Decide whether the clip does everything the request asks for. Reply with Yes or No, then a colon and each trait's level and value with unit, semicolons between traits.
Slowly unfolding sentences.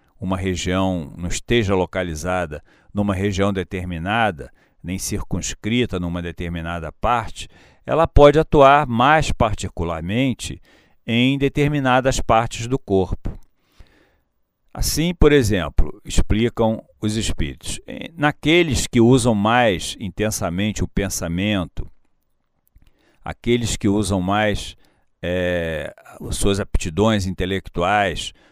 Yes: slow, 95 wpm